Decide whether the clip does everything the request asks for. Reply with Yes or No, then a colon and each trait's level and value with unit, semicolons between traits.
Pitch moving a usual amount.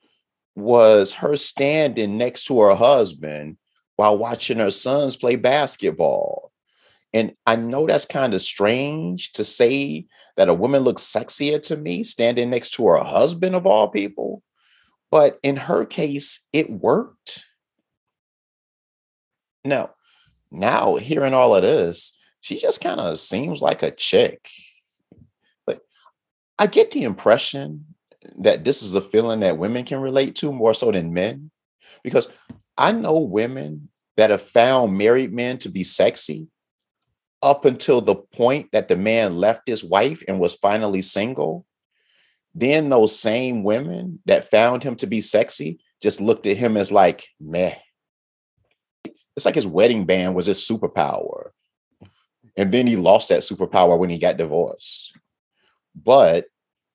No: wide, 7.5 semitones